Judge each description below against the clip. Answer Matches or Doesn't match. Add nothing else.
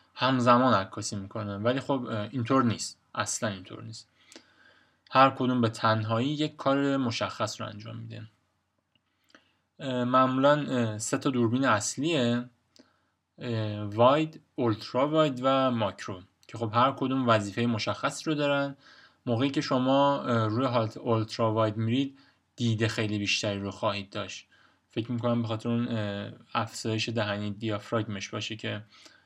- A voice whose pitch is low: Matches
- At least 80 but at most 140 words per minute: Matches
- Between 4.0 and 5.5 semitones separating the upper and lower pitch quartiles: Doesn't match